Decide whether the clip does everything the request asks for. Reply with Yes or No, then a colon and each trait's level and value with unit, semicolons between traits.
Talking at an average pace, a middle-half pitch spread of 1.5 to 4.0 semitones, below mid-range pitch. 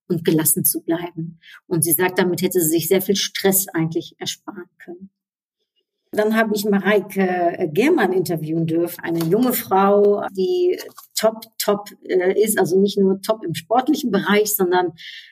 No: average, 155 wpm; average, 3.1 semitones; high, 195 Hz